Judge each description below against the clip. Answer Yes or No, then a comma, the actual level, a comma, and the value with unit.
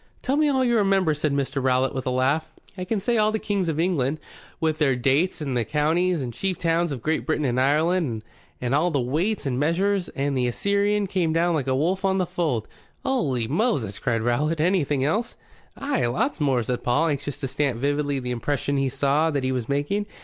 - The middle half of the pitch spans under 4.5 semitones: No, wide, 5.6 semitones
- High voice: No, medium, 150 Hz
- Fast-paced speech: Yes, fast, 220 wpm